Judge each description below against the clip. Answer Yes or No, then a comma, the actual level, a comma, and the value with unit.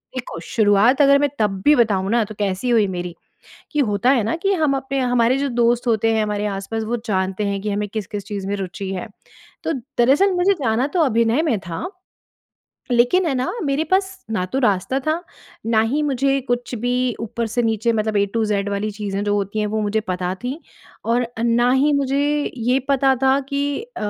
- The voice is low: No, high, 230 Hz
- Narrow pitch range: No, average, 4.6 semitones